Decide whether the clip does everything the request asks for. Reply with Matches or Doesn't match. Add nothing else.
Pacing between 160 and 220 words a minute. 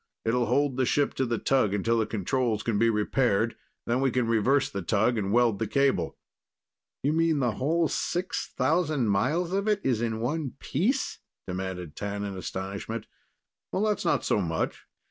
Matches